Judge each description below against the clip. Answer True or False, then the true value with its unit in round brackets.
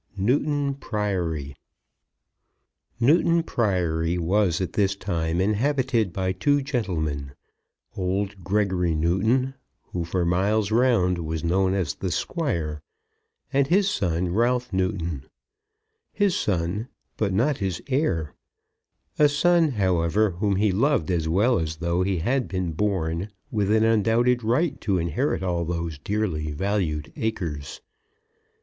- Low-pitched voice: True (95 Hz)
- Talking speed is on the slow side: True (125 wpm)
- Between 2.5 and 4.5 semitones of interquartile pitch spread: False (5.5 semitones)